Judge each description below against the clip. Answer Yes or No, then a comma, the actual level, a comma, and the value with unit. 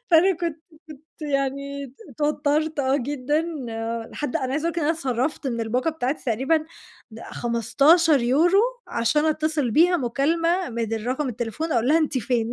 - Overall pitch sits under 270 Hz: No, very high, 280 Hz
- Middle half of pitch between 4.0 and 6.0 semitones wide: Yes, average, 4.3 semitones